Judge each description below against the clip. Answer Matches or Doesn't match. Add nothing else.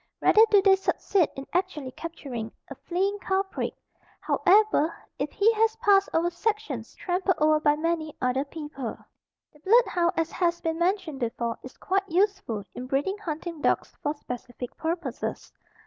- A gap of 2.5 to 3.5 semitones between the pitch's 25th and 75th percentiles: Doesn't match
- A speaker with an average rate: Matches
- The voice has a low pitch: Doesn't match